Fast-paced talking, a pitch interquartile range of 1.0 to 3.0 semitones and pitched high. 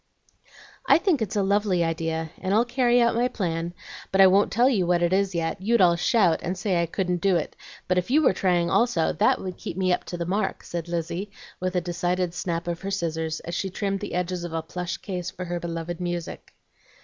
No: fast, 230 wpm; narrow, 2.4 semitones; medium, 180 Hz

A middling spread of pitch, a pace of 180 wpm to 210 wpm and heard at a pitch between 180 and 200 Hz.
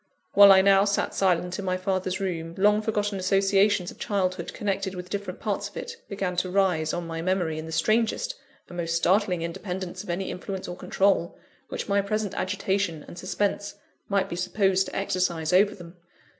No: narrow, 2.0 semitones; average, 185 wpm; high, 190 Hz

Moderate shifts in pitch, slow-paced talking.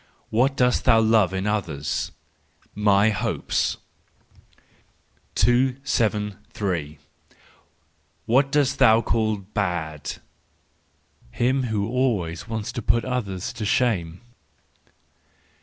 Yes: average, 4.2 semitones; slow, 90 wpm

